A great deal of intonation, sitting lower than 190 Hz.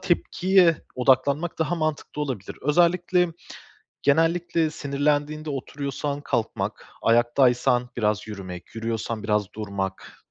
Yes: wide, 5.7 semitones; medium, 140 Hz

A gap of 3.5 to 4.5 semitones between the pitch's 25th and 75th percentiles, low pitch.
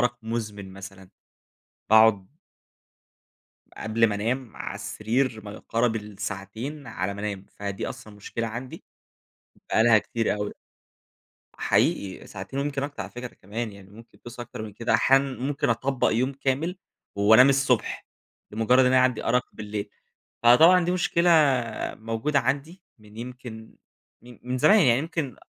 Yes: average, 3.9 semitones; low, 115 Hz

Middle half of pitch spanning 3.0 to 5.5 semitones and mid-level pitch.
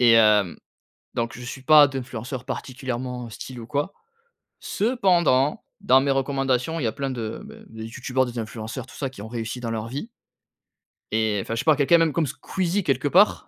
No: average, 3.9 semitones; low, 130 Hz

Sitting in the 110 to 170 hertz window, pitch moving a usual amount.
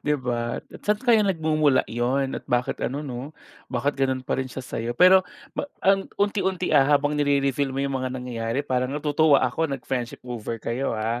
Yes: low, 135 Hz; average, 3.4 semitones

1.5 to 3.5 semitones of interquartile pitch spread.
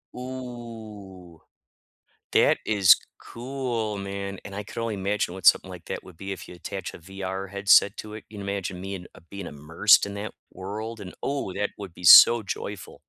Yes: narrow, 2.4 semitones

